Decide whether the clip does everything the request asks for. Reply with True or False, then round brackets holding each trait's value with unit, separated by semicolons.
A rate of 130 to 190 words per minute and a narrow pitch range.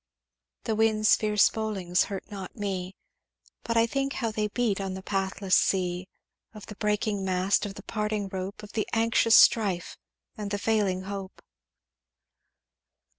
True (150 wpm; 2.3 semitones)